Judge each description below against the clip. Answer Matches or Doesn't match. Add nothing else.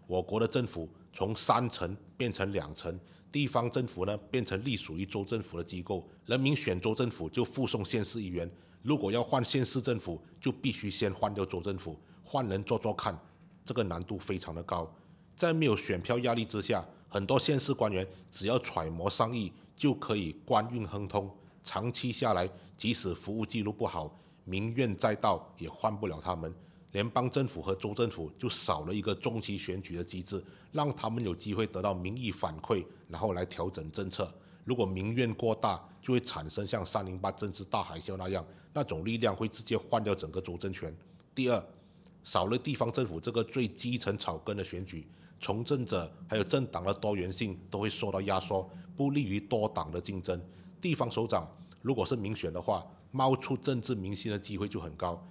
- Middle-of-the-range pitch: Doesn't match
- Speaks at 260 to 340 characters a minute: Matches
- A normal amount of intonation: Matches